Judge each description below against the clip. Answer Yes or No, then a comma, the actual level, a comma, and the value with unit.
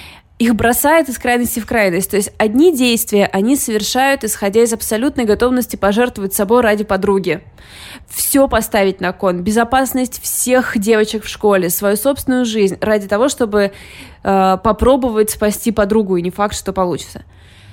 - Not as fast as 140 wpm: No, average, 150 wpm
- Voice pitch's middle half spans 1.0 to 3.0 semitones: No, average, 3.5 semitones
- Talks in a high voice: Yes, high, 220 Hz